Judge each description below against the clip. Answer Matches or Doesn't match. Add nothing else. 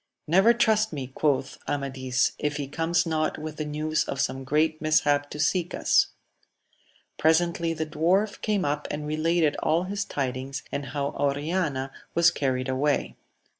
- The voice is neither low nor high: Matches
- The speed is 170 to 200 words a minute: Doesn't match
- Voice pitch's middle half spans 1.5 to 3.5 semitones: Matches